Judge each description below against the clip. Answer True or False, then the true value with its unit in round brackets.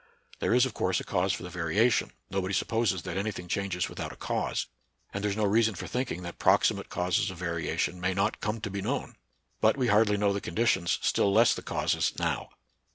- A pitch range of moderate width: True (3.2 semitones)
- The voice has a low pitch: True (100 Hz)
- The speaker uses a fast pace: True (220 wpm)